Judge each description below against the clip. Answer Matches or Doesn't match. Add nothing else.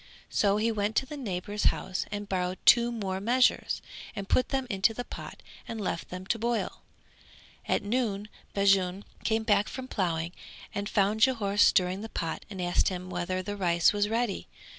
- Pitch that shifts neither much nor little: Matches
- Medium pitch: Doesn't match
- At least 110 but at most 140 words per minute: Doesn't match